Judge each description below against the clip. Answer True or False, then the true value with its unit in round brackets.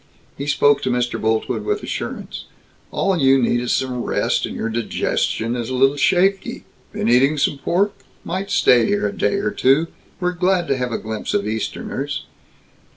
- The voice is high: False (135 Hz)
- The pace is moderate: True (180 wpm)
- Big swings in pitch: True (6.8 semitones)